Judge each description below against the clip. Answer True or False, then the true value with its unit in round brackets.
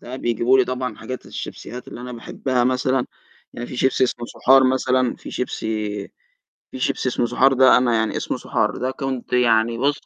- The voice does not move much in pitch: True (1.4 semitones)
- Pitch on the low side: True (125 Hz)